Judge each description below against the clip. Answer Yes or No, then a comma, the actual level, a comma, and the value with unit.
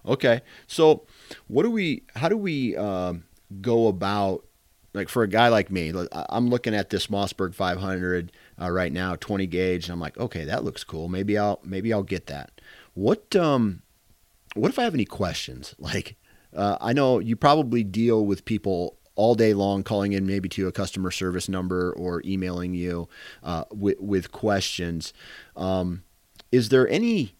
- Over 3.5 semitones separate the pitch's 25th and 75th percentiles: Yes, average, 3.9 semitones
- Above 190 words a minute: No, average, 175 wpm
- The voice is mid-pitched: No, very low, 95 Hz